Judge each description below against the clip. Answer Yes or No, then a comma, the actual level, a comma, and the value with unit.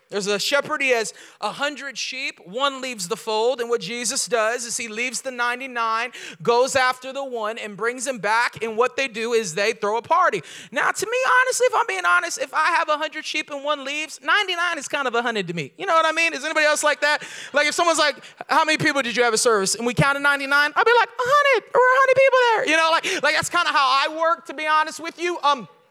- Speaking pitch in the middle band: No, very high, 285 Hz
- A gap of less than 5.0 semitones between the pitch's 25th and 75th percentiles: No, wide, 5.5 semitones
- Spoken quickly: Yes, fast, 265 wpm